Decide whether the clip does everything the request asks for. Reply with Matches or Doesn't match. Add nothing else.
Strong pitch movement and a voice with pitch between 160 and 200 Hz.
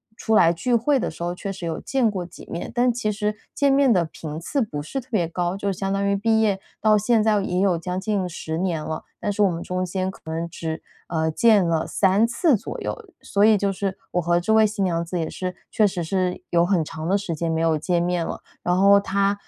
Doesn't match